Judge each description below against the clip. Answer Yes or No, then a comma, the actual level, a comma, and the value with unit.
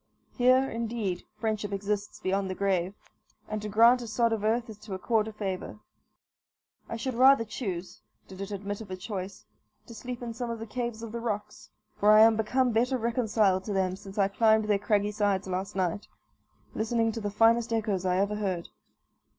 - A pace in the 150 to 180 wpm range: No, average, 195 wpm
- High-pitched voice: Yes, high, 215 Hz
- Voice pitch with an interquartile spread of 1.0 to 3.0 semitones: Yes, narrow, 2.6 semitones